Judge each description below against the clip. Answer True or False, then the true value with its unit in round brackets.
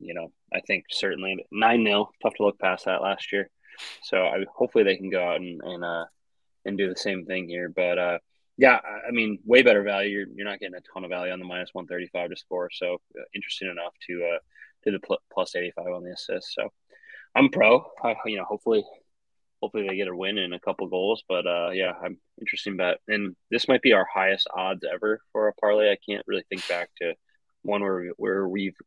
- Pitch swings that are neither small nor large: True (3.4 semitones)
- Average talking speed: False (230 wpm)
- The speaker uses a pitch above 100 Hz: False (95 Hz)